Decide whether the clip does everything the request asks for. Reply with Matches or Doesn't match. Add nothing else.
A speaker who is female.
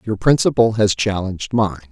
Doesn't match